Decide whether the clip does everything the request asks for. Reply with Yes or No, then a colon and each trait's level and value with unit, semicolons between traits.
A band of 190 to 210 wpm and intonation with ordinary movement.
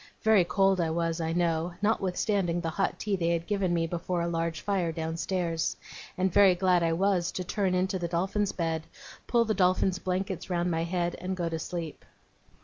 No: average, 195 wpm; narrow, 2.2 semitones